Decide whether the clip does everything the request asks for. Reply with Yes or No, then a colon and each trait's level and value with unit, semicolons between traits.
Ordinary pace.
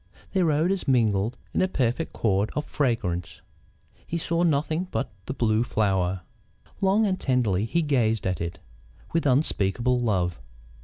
Yes: average, 145 wpm